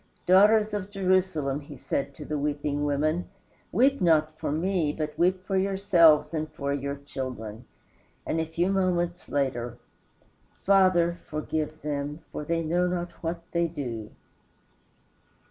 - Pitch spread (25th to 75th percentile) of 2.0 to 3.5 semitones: No, average, 4.0 semitones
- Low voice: No, medium, 160 Hz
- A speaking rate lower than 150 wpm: Yes, average, 140 wpm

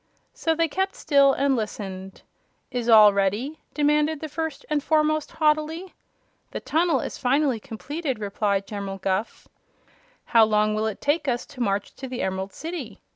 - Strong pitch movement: Yes, wide, 6.5 semitones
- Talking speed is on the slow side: No, average, 160 wpm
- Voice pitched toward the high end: Yes, very high, 265 Hz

